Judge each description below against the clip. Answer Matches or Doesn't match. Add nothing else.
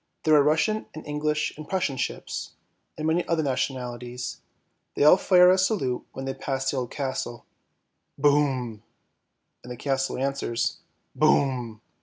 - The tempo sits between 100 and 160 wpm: Matches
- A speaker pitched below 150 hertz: Matches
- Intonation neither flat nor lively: Matches